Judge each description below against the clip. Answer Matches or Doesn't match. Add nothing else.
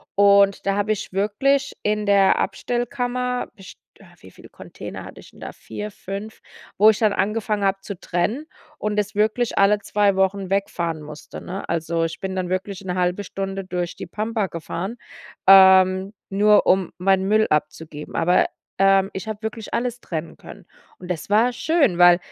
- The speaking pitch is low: Doesn't match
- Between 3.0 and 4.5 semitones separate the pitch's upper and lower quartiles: Doesn't match